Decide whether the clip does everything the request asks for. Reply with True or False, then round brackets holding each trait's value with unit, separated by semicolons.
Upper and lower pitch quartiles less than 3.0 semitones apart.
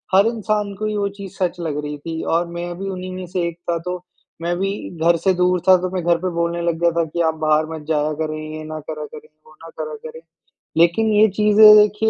False (3.4 semitones)